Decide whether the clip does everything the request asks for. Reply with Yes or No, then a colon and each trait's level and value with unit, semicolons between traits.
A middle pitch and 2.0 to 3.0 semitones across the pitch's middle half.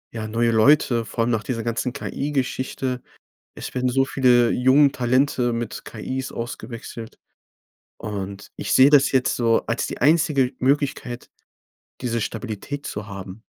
No: low, 125 Hz; average, 2.7 semitones